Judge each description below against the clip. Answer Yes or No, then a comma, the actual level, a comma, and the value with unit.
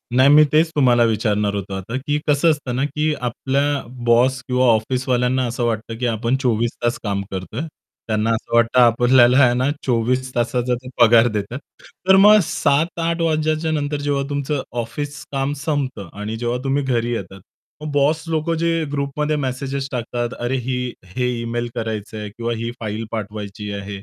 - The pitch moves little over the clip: No, average, 3.8 semitones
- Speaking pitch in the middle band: No, low, 125 Hz